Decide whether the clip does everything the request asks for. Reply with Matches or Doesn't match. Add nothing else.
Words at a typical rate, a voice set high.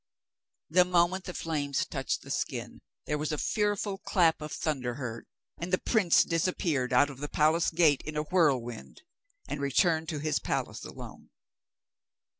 Doesn't match